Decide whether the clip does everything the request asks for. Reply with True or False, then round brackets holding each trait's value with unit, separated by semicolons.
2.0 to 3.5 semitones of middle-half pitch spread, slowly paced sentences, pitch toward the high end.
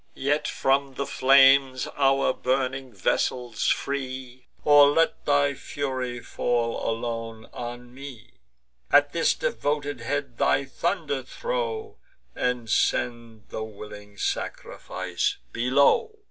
False (3.1 semitones; 105 wpm; 130 Hz)